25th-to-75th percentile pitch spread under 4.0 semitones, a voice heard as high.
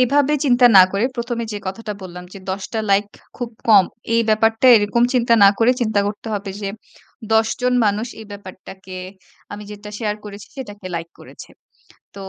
Yes: average, 2.9 semitones; high, 210 Hz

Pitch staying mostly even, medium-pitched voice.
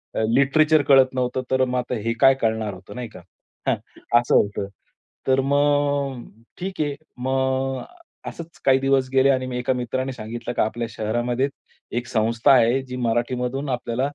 No: narrow, 2.1 semitones; low, 130 Hz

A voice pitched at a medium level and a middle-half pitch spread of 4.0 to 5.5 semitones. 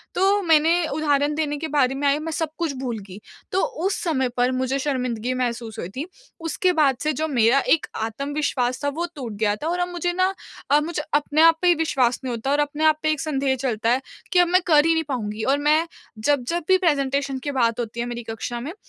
No: very high, 285 Hz; average, 4.4 semitones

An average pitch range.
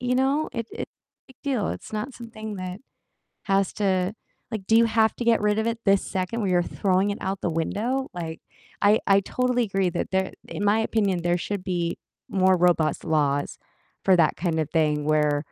Yes: average, 4.1 semitones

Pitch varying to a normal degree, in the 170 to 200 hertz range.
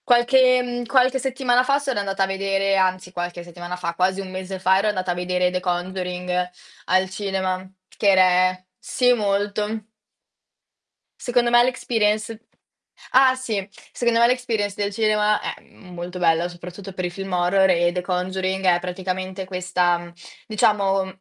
Yes: average, 3.1 semitones; high, 190 Hz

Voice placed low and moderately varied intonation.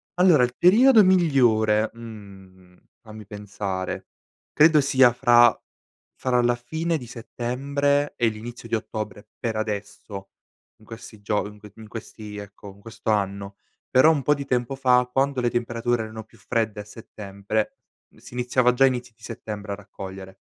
Yes: low, 115 Hz; average, 3.4 semitones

